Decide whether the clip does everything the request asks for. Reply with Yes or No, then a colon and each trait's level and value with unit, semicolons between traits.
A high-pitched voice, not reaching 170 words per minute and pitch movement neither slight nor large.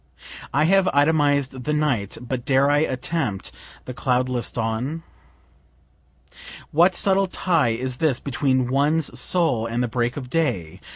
No: low, 135 Hz; slow, 135 wpm; average, 4.0 semitones